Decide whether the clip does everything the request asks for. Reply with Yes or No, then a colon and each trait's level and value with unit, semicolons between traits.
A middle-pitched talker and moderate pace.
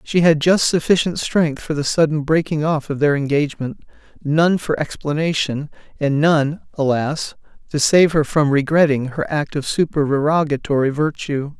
Yes: medium, 150 Hz; average, 150 wpm